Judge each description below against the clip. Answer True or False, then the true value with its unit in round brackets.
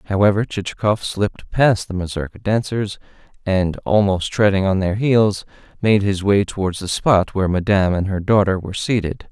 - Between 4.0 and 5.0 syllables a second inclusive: False (5.2 syllables/s)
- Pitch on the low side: True (100 Hz)